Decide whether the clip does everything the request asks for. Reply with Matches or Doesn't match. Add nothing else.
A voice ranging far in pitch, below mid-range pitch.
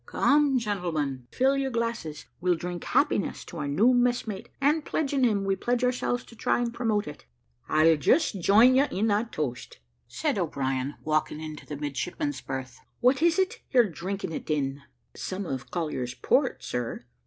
Doesn't match